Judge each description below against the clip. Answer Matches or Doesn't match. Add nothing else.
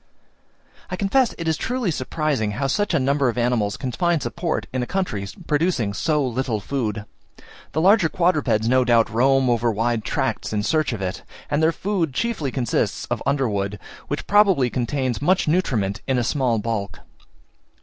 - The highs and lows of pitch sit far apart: Matches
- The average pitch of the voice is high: Doesn't match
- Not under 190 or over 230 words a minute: Doesn't match